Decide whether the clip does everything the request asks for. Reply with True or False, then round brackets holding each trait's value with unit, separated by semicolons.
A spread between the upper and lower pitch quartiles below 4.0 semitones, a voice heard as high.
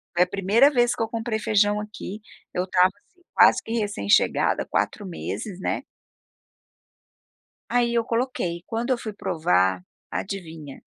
False (4.4 semitones; 205 Hz)